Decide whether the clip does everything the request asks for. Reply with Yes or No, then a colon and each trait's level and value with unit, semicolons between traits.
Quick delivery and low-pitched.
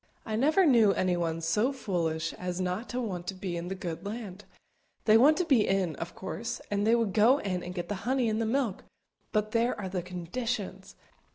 No: fast, 210 wpm; high, 200 Hz